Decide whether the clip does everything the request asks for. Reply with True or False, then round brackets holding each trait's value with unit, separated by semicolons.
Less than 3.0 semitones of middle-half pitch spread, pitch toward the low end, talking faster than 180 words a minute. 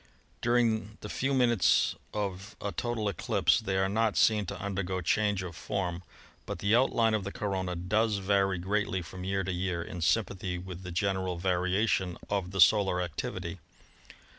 False (2.6 semitones; 95 Hz; 165 wpm)